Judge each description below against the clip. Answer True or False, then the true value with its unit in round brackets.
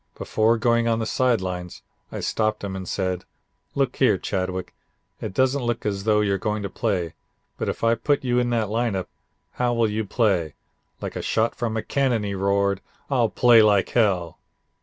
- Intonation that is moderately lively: True (3.2 semitones)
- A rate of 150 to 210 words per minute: True (190 wpm)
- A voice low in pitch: True (110 Hz)